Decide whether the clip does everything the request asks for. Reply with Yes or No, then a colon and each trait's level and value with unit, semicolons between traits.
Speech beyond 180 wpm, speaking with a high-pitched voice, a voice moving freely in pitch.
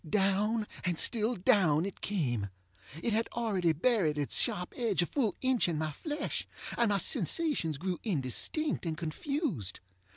No: average, 155 wpm; high, 195 Hz; wide, 6.6 semitones